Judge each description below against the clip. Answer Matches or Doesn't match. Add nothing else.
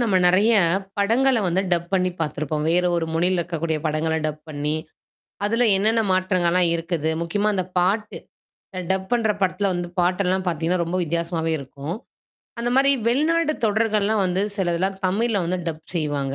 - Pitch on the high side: Doesn't match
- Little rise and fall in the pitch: Doesn't match